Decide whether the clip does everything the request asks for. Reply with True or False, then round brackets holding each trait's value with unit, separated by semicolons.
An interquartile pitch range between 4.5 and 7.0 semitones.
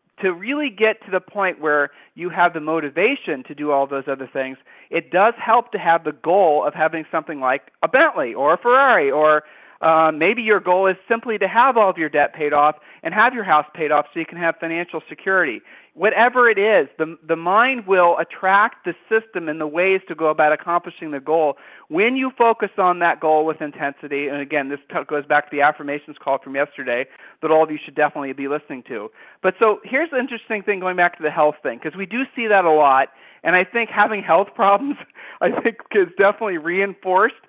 True (5.3 semitones)